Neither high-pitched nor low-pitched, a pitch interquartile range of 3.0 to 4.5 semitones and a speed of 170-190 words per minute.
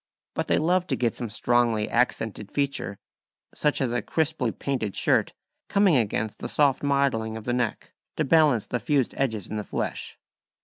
No: low, 125 Hz; average, 4.2 semitones; average, 175 wpm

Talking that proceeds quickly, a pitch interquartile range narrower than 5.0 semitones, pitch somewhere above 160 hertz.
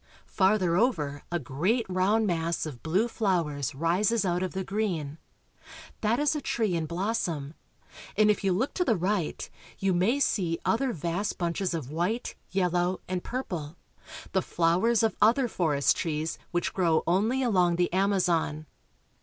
No: average, 155 wpm; average, 4.3 semitones; medium, 185 Hz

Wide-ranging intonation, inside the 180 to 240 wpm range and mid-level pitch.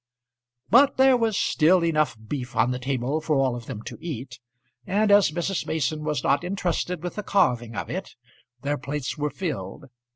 Yes: wide, 5.8 semitones; average, 185 wpm; medium, 150 Hz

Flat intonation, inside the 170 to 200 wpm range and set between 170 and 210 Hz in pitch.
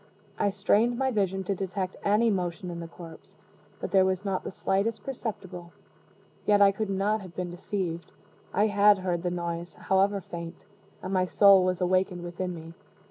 Yes: narrow, 2.3 semitones; average, 180 wpm; high, 190 Hz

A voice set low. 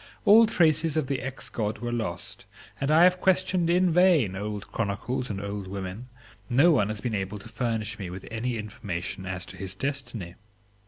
Yes: low, 115 Hz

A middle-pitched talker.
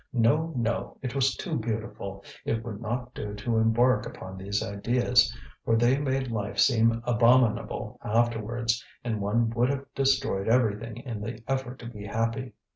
No: low, 115 Hz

